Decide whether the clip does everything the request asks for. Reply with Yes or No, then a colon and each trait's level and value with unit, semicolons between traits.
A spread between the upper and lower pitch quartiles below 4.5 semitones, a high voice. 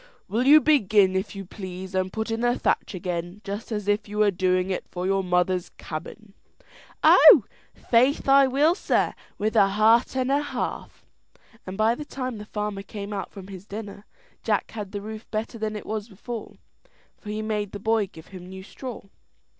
Yes: average, 3.0 semitones; high, 210 Hz